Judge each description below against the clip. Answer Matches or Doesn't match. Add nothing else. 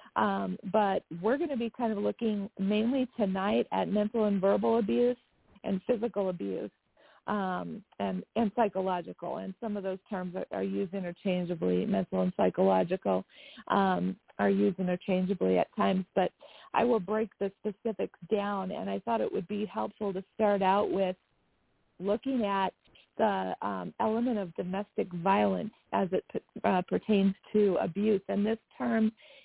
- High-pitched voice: Matches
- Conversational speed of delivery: Matches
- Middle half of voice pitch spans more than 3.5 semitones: Doesn't match